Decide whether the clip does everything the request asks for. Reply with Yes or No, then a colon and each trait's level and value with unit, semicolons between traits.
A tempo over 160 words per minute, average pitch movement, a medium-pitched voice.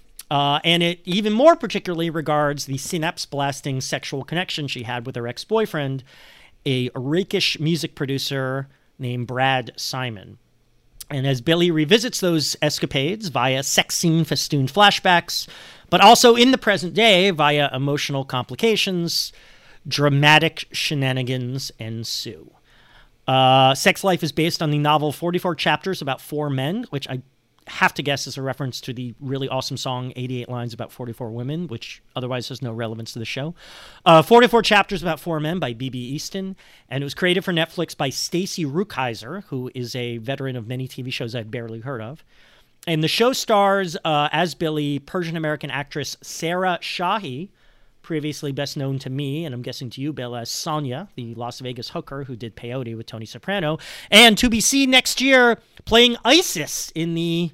Yes: average, 170 wpm; average, 5.0 semitones; medium, 145 Hz